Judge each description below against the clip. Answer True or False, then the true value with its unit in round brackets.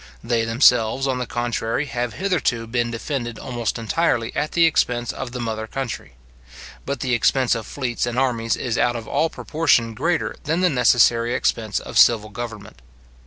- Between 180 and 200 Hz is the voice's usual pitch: False (120 Hz)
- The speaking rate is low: False (170 wpm)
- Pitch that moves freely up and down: False (2.7 semitones)